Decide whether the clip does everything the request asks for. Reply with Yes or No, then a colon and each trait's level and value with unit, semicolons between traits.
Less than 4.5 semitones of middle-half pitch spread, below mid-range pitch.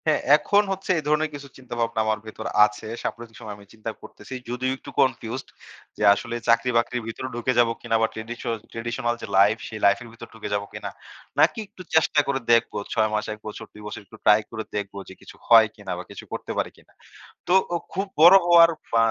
Yes: average, 3.4 semitones; low, 115 Hz